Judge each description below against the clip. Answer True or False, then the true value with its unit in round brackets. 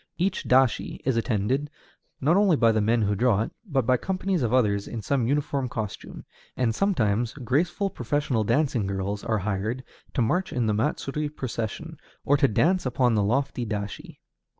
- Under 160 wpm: False (175 wpm)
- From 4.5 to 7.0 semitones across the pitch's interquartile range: True (5.0 semitones)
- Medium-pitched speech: False (125 Hz)